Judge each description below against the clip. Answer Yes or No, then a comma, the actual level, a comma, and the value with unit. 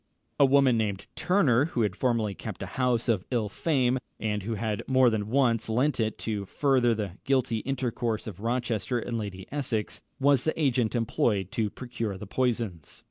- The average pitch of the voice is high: No, low, 115 Hz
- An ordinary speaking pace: Yes, average, 180 wpm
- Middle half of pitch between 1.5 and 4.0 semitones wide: Yes, average, 3.4 semitones